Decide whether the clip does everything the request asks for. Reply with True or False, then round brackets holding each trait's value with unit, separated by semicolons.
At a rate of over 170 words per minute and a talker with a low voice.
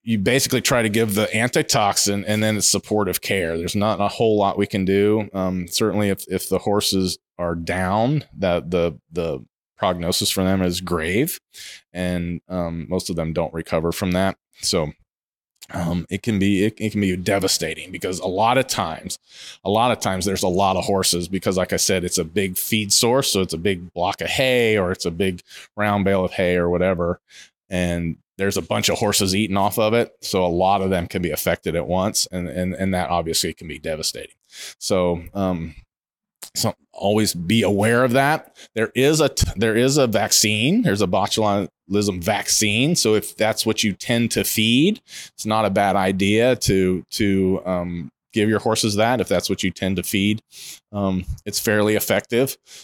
True (200 wpm; 100 Hz)